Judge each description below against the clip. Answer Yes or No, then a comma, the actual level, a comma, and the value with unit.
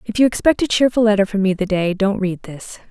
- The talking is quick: Yes, fast, 270 wpm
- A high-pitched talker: Yes, high, 205 Hz